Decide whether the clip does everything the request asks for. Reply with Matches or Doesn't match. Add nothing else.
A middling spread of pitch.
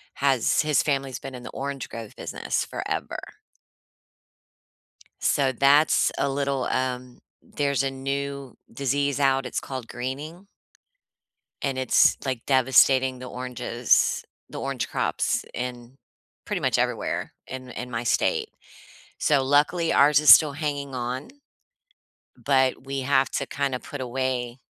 Doesn't match